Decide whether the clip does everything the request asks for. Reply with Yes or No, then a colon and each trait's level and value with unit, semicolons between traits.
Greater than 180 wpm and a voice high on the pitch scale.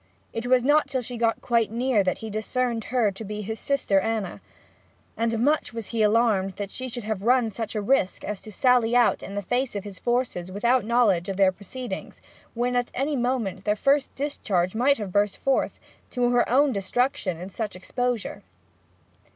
Yes: average, 190 wpm; high, 230 Hz